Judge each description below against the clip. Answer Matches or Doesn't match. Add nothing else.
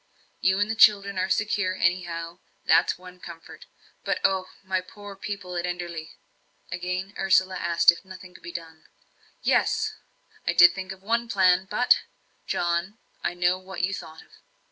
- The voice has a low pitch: Doesn't match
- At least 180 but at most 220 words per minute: Doesn't match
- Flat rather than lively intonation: Matches